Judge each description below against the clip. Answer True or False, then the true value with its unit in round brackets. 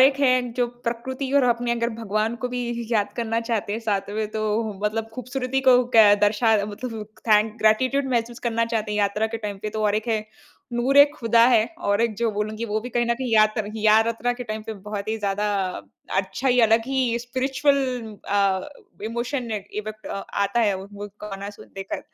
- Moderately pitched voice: False (225 Hz)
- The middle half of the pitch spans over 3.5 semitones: False (2.4 semitones)